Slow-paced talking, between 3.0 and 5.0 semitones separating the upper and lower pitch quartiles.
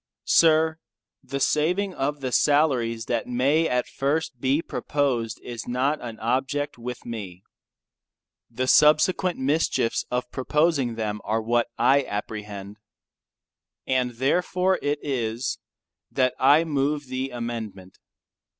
Yes: slow, 120 wpm; average, 4.1 semitones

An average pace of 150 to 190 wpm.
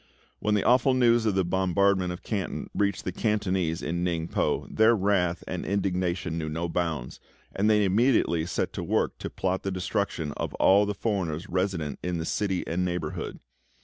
Yes: average, 180 wpm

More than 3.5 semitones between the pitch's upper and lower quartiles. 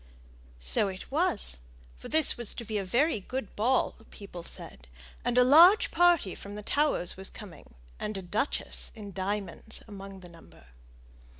Yes: wide, 5.4 semitones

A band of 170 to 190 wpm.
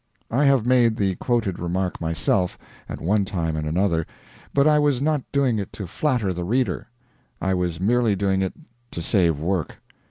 Yes: average, 180 wpm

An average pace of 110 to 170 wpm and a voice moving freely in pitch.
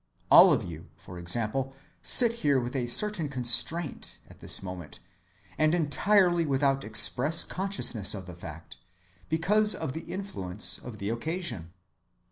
Yes: average, 140 wpm; wide, 8.9 semitones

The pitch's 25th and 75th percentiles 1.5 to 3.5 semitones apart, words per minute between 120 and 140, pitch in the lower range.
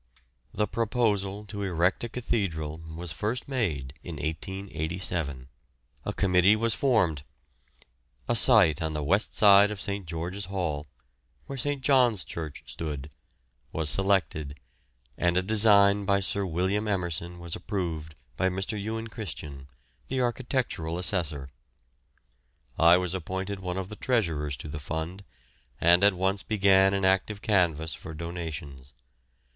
No: average, 4.2 semitones; slow, 135 wpm; very low, 95 Hz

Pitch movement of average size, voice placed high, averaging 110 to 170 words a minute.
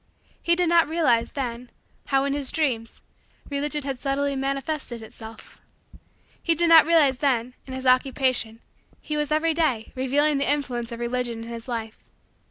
Yes: average, 3.9 semitones; very high, 270 Hz; average, 165 wpm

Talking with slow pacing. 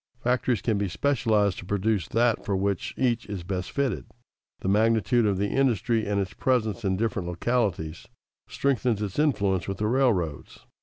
No: average, 165 wpm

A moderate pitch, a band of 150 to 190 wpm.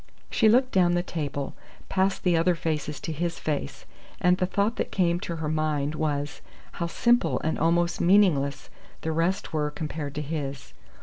Yes: medium, 165 Hz; average, 175 wpm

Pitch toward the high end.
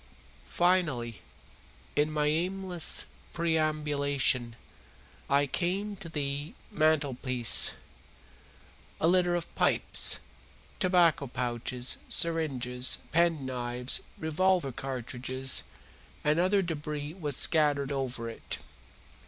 No: medium, 150 Hz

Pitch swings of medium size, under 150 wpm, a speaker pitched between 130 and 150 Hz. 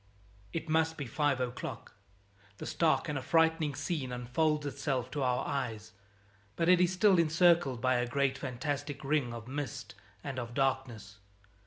No: average, 4.2 semitones; average, 155 wpm; medium, 140 Hz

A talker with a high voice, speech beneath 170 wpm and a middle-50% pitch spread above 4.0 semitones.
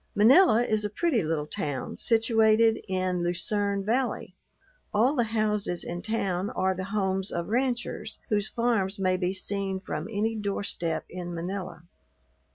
No: high, 200 Hz; average, 145 wpm; average, 3.3 semitones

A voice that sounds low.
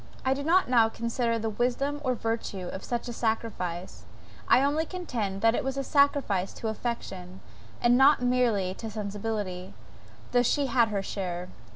No: high, 230 Hz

